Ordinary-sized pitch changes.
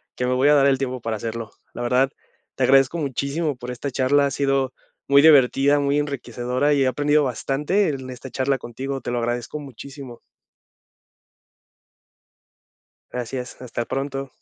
No: narrow, 2.2 semitones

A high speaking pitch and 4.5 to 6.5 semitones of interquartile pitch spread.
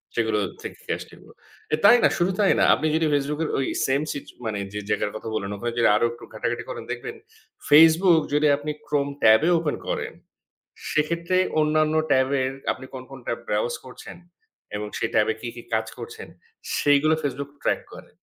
No: medium, 140 Hz; average, 4.8 semitones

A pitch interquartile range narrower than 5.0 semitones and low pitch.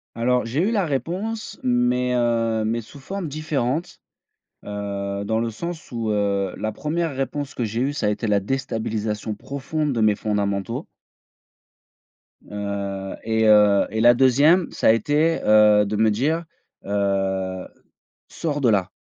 No: wide, 5.4 semitones; low, 115 Hz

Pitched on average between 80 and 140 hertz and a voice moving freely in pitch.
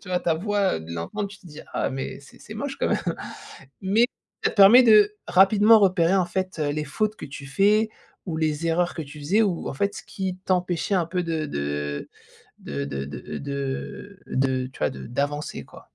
No: medium, 175 Hz; wide, 6.2 semitones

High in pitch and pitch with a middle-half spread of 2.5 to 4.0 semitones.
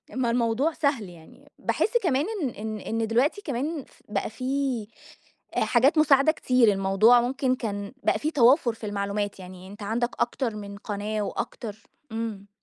No: high, 230 Hz; average, 4.6 semitones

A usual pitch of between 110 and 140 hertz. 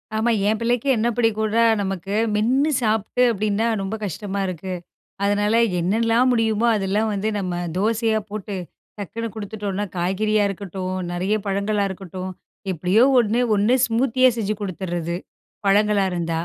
No: high, 210 Hz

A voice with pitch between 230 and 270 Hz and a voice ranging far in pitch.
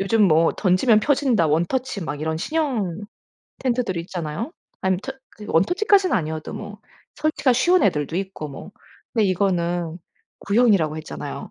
No: high, 195 Hz; wide, 7.1 semitones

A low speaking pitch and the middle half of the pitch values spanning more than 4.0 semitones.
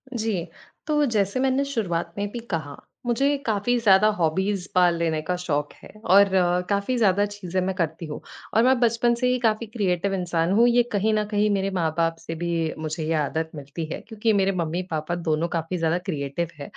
No: medium, 185 Hz; average, 4.7 semitones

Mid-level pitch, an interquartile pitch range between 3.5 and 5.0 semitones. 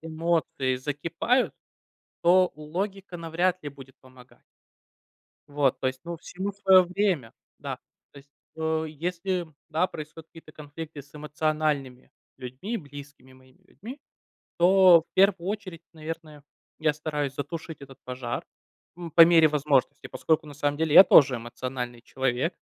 Yes: medium, 155 Hz; average, 3.8 semitones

